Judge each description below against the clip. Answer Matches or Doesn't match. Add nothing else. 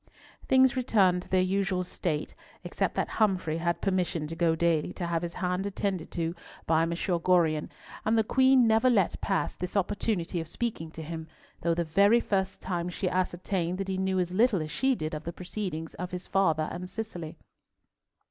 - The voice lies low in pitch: Doesn't match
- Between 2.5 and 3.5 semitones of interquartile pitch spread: Matches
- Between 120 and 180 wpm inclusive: Doesn't match